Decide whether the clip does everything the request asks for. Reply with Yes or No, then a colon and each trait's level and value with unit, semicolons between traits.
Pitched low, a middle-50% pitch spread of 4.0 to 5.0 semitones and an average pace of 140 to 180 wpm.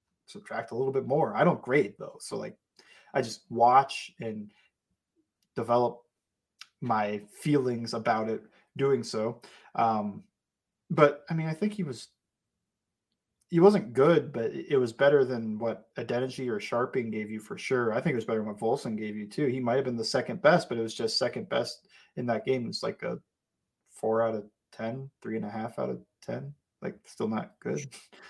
No: low, 120 Hz; average, 4.6 semitones; average, 190 wpm